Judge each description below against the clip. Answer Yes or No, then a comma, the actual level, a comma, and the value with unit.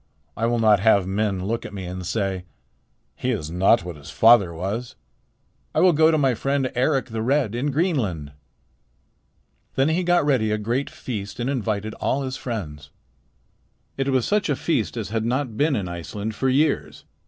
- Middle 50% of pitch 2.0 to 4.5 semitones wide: No, average, 5.3 semitones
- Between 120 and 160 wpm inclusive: No, average, 185 wpm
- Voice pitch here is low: Yes, low, 115 Hz